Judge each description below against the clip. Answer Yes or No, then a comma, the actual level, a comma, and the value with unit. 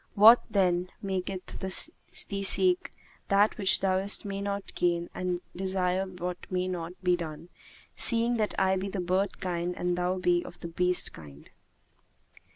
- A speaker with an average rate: Yes, average, 160 wpm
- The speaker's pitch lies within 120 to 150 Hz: No, medium, 185 Hz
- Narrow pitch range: Yes, narrow, 1.8 semitones